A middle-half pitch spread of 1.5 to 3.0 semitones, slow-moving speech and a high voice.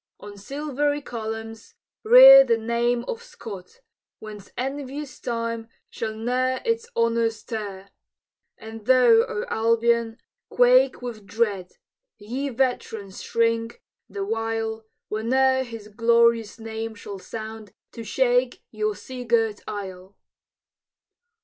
Yes: narrow, 2.6 semitones; slow, 110 wpm; high, 230 Hz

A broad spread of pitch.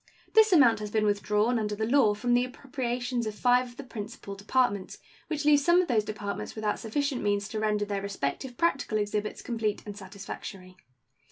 No: average, 3.5 semitones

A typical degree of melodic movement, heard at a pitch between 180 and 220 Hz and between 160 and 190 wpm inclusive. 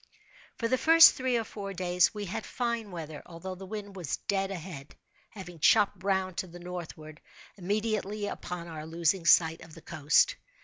Yes: average, 3.7 semitones; medium, 185 Hz; average, 175 wpm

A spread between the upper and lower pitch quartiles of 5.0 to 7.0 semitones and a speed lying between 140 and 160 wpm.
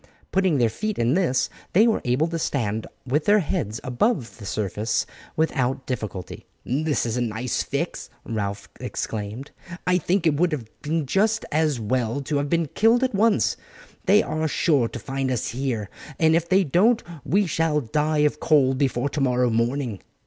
No: wide, 5.6 semitones; average, 175 wpm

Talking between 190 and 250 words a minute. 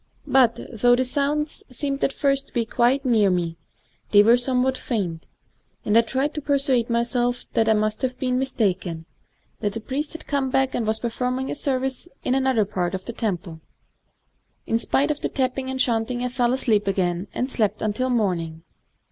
Yes: average, 200 wpm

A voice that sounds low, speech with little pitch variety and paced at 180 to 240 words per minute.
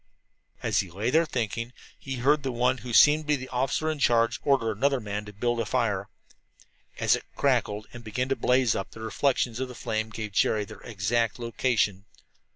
No: low, 120 Hz; average, 3.3 semitones; average, 200 wpm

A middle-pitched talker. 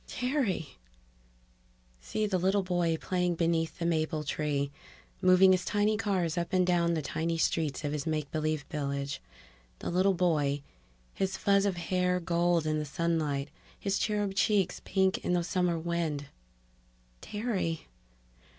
Yes: medium, 170 Hz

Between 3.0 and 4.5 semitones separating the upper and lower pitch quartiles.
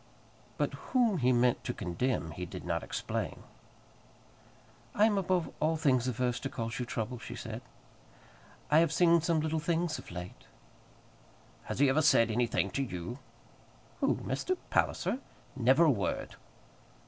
No: wide, 5.6 semitones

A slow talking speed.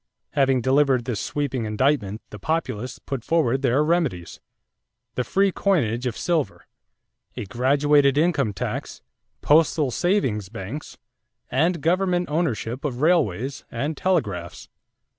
Yes: slow, 120 wpm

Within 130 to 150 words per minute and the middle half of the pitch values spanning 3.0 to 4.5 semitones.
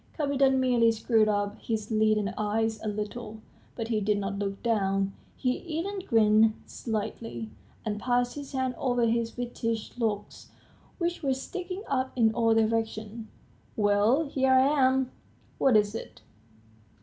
Yes: average, 145 wpm; average, 3.5 semitones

